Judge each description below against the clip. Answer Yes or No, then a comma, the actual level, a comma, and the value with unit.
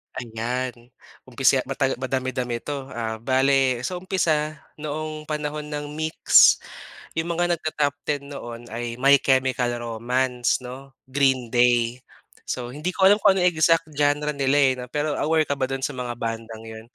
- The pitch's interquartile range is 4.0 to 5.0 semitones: No, average, 3.5 semitones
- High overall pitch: No, low, 135 Hz